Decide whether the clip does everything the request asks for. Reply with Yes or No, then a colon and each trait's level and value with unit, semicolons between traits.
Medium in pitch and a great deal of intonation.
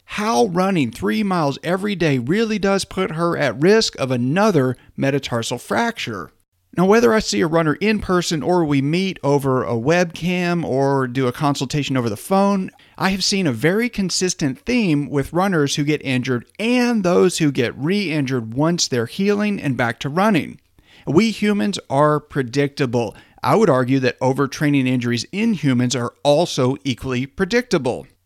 Yes: medium, 150 Hz; wide, 6.5 semitones